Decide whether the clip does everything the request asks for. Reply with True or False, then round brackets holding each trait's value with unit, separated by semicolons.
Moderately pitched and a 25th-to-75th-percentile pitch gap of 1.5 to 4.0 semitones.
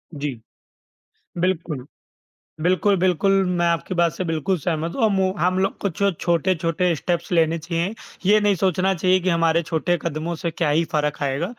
True (170 Hz; 2.4 semitones)